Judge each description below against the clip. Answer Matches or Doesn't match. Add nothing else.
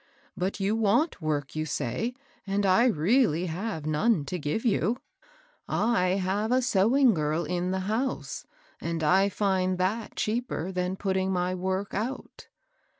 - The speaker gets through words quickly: Doesn't match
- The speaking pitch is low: Doesn't match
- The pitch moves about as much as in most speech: Matches